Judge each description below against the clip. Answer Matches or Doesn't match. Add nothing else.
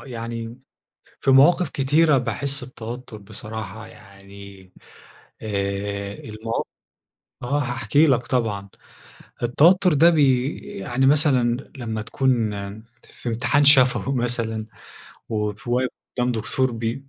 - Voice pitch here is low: Matches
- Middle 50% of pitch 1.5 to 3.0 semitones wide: Doesn't match